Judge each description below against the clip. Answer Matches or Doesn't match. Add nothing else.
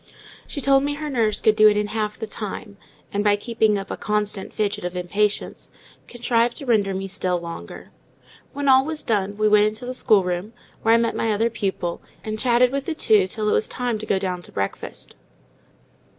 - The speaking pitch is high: Matches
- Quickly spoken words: Matches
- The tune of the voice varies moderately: Matches